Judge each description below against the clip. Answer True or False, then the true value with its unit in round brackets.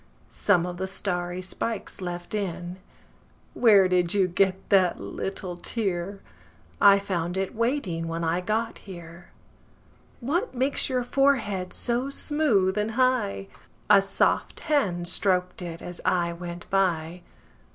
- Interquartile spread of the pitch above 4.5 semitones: False (3.4 semitones)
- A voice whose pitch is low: False (185 Hz)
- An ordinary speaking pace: False (120 wpm)